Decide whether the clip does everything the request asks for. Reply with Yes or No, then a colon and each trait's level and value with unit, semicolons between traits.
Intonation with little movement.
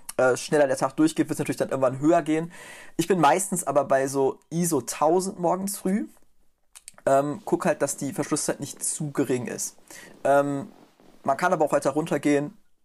No: average, 3.6 semitones